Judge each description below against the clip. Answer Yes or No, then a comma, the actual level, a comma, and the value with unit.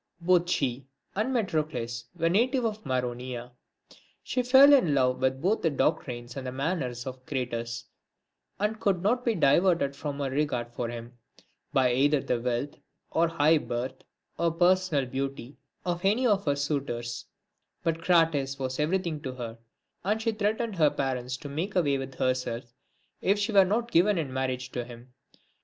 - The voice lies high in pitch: No, medium, 140 Hz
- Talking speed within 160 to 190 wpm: Yes, average, 165 wpm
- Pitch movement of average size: No, wide, 6.4 semitones